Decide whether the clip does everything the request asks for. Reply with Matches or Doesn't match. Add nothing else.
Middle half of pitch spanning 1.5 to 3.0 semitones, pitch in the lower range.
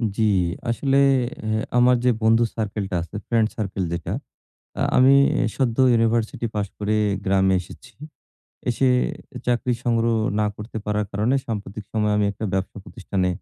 Matches